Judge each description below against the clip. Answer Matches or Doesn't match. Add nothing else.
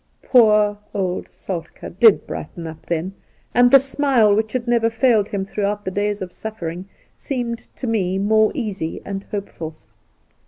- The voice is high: Matches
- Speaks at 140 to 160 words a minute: Matches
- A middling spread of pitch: Matches